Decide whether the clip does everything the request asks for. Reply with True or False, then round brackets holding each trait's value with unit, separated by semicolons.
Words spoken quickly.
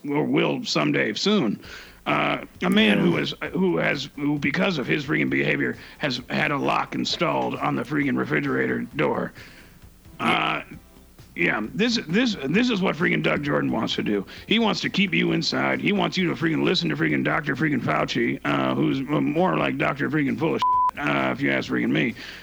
False (185 wpm)